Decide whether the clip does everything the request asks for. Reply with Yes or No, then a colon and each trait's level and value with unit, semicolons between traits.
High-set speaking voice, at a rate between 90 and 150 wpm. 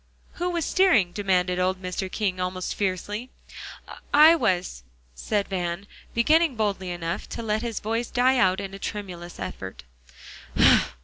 Yes: high, 200 Hz; average, 140 wpm